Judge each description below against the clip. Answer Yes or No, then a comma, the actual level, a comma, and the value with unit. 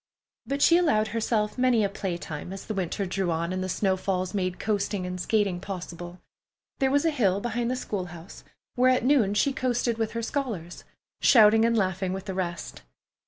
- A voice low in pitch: No, high, 200 Hz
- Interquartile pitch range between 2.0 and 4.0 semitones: No, average, 4.4 semitones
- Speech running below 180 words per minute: No, average, 195 wpm